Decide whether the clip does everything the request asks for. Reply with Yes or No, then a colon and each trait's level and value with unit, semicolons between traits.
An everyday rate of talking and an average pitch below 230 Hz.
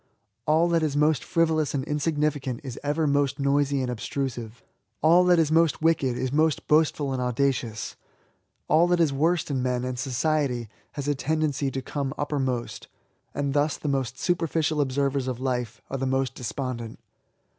Yes: average, 165 wpm; medium, 140 Hz